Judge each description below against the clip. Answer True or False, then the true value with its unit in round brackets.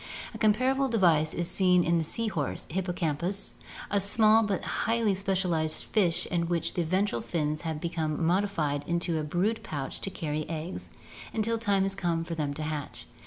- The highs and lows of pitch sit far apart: False (4.2 semitones)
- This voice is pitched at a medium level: True (175 Hz)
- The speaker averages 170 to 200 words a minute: True (180 wpm)